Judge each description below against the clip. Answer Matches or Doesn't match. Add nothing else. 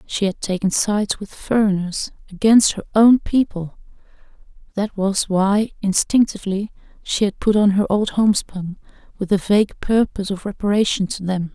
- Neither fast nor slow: Matches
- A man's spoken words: Doesn't match